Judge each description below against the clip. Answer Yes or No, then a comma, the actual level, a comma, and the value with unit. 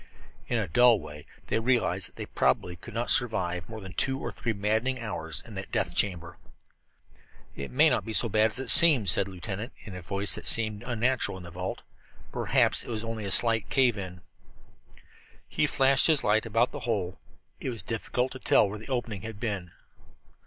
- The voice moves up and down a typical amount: Yes, average, 4.2 semitones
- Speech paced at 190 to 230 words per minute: Yes, average, 200 wpm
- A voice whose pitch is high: No, low, 110 Hz